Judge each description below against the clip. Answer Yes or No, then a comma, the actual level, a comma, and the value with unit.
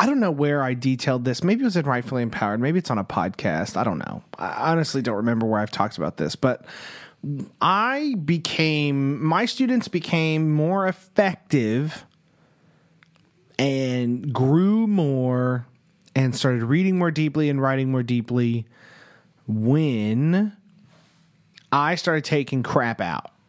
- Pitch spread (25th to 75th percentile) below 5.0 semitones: No, average, 5.3 semitones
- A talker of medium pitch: Yes, medium, 145 Hz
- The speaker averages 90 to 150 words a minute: Yes, average, 145 wpm